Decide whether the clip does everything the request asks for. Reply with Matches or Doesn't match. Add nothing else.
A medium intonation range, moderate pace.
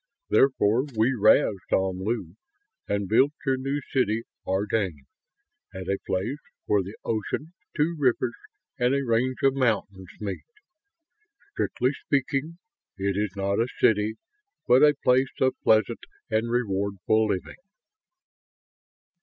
Doesn't match